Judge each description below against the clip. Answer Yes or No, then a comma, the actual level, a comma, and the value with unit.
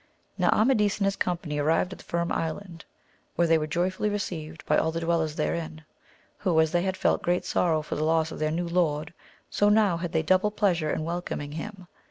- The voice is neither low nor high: Yes, medium, 170 Hz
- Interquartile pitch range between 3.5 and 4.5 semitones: No, average, 2.9 semitones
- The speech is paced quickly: Yes, fast, 215 wpm